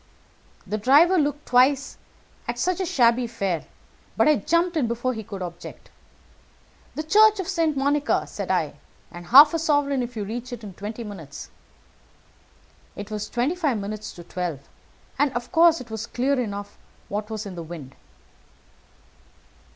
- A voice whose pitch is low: No, high, 240 Hz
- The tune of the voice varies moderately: No, wide, 6.4 semitones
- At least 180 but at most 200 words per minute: No, average, 165 wpm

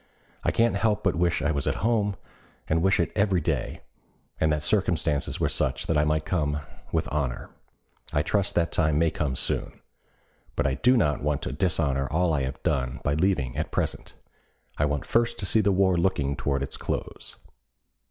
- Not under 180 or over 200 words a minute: Yes, average, 190 wpm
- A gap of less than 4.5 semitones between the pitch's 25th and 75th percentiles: No, average, 4.8 semitones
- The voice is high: No, very low, 80 Hz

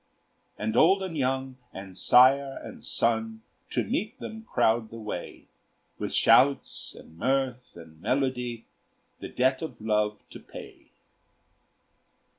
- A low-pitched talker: Yes, low, 125 Hz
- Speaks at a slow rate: Yes, slow, 125 wpm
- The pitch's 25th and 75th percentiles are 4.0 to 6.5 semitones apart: No, average, 3.6 semitones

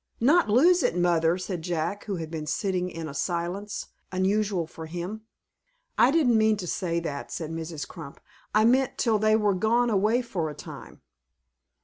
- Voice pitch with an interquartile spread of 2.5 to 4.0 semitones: No, average, 4.7 semitones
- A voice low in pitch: No, medium, 185 Hz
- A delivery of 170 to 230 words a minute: Yes, average, 175 wpm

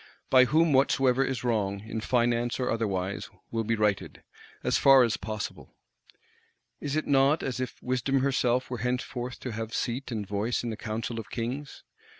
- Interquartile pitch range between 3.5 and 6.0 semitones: No, average, 2.8 semitones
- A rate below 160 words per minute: No, average, 165 wpm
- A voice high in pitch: No, low, 120 Hz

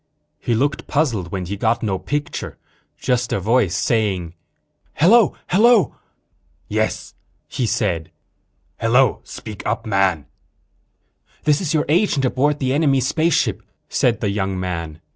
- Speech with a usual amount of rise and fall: No, wide, 7.2 semitones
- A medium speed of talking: No, slow, 130 wpm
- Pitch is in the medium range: No, low, 120 Hz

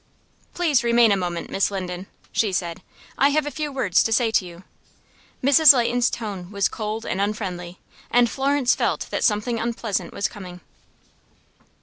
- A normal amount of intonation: Yes, average, 4.7 semitones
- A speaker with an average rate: Yes, average, 160 wpm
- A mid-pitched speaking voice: No, high, 215 Hz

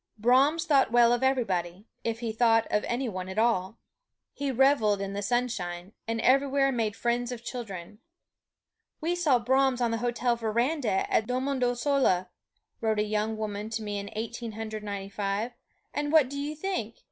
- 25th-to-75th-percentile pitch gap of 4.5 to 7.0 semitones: No, average, 3.8 semitones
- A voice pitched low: No, high, 230 Hz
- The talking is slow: No, average, 170 wpm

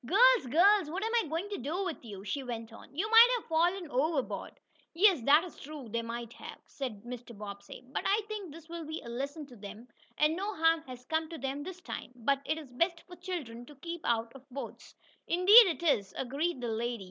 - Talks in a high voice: Yes, very high, 300 Hz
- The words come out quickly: Yes, fast, 225 wpm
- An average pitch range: No, wide, 6.3 semitones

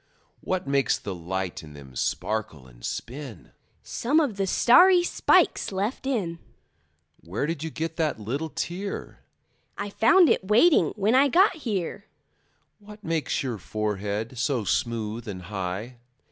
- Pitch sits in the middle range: Yes, medium, 150 Hz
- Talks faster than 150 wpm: No, average, 145 wpm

